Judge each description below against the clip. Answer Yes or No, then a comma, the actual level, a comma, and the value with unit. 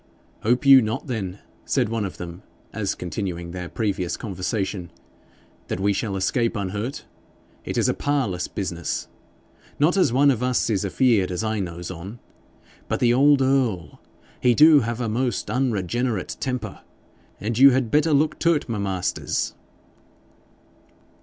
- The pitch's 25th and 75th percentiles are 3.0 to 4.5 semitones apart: No, wide, 5.5 semitones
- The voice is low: Yes, low, 110 Hz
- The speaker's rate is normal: Yes, average, 145 wpm